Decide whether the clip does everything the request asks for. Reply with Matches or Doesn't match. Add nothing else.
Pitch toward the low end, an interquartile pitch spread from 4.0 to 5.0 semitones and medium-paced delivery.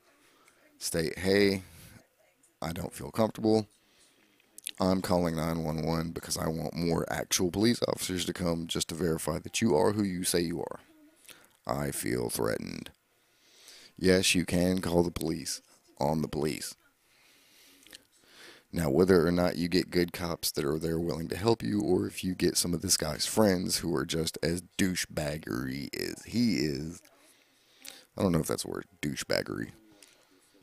Doesn't match